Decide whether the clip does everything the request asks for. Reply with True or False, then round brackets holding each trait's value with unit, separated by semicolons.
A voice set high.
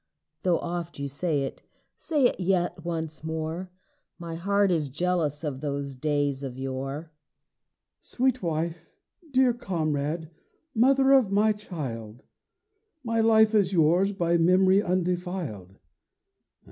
False (170 Hz)